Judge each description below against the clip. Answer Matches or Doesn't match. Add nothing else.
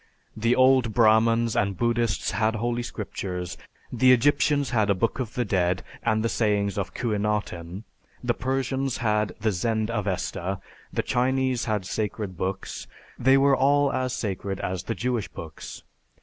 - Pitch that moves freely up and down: Doesn't match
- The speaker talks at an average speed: Matches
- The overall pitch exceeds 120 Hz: Doesn't match